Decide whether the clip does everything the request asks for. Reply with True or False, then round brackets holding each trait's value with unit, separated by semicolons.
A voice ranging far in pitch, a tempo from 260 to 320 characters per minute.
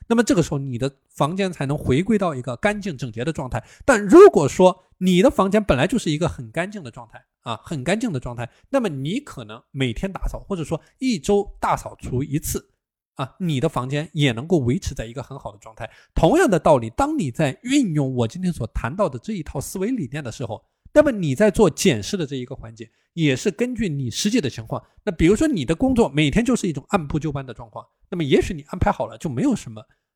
False (7.8 semitones; 345 characters per minute)